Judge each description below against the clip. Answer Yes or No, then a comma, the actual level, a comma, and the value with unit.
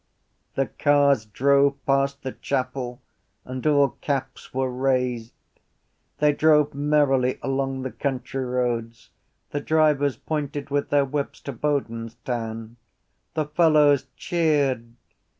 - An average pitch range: No, narrow, 2.3 semitones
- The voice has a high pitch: No, low, 135 Hz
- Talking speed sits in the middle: No, slow, 115 wpm